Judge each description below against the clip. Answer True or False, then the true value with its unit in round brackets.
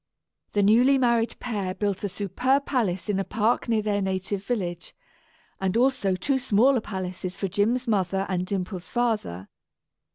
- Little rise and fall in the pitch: False (4.1 semitones)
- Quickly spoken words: False (155 wpm)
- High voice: True (205 Hz)